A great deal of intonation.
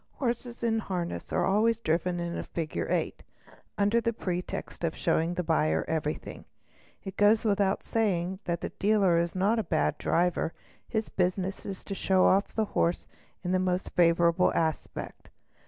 No: average, 3.3 semitones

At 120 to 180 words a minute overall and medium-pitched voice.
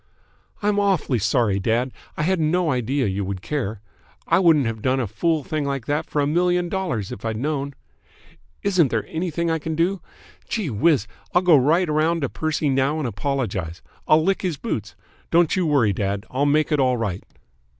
No: average, 190 wpm; medium, 145 Hz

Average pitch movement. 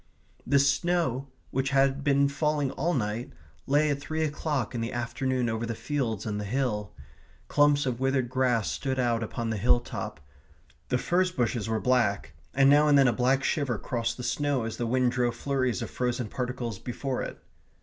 Yes: average, 3.1 semitones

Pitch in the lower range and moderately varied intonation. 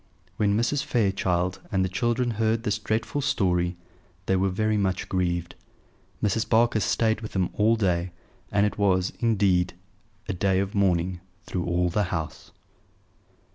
Yes: low, 100 Hz; average, 3.3 semitones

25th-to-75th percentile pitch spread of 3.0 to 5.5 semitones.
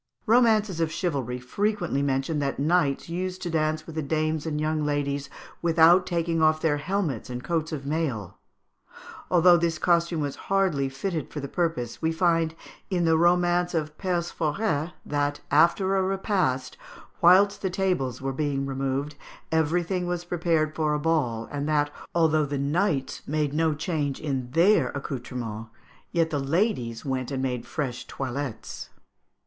Yes: average, 3.8 semitones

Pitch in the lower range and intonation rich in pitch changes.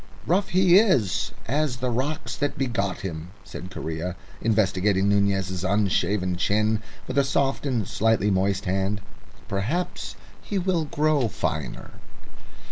Yes: low, 105 Hz; wide, 6.7 semitones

